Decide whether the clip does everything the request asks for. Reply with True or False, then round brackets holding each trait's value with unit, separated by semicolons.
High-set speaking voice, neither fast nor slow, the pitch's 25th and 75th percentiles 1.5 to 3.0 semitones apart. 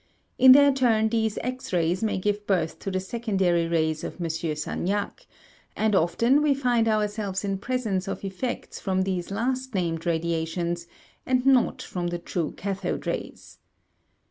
False (195 Hz; 155 wpm; 5.1 semitones)